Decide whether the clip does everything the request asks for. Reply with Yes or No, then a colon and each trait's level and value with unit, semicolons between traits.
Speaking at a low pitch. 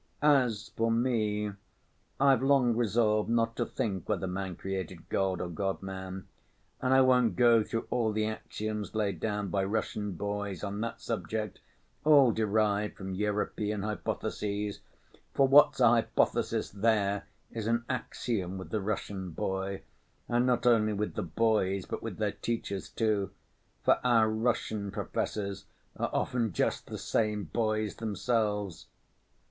Yes: low, 105 Hz